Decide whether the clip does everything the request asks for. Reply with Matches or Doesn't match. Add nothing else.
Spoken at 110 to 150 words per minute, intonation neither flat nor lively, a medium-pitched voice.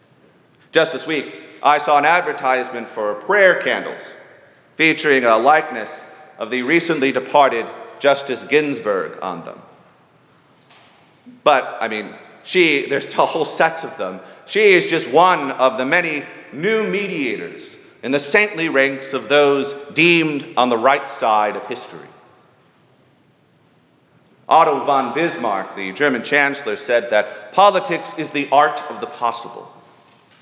Matches